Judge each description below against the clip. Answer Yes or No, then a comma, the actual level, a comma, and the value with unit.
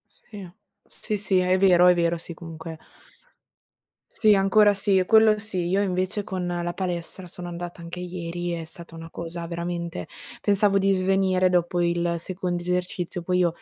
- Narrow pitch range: Yes, narrow, 1.9 semitones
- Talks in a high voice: No, medium, 180 Hz